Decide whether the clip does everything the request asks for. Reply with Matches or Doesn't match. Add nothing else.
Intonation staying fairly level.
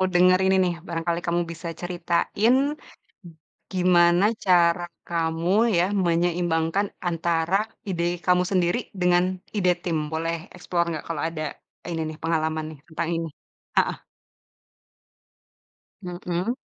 Matches